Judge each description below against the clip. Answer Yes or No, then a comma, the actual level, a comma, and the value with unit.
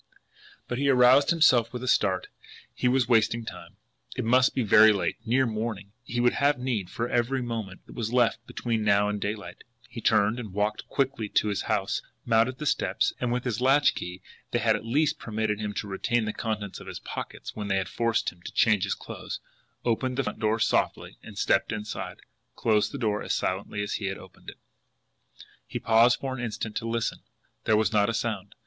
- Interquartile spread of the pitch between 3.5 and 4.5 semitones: No, average, 2.8 semitones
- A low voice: Yes, low, 115 Hz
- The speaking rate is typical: No, fast, 210 wpm